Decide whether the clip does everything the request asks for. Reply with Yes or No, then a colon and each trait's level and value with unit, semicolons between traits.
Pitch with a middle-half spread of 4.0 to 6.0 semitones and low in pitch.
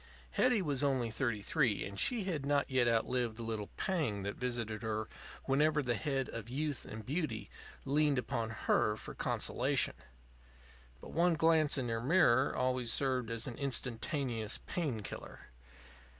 Yes: average, 4.5 semitones; low, 130 Hz